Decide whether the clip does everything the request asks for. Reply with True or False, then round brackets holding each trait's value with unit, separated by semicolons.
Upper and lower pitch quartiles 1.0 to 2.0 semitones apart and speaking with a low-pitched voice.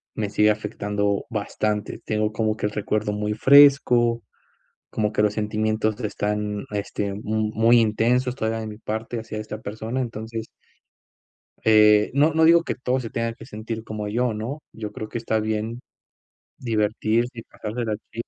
True (1.7 semitones; 110 Hz)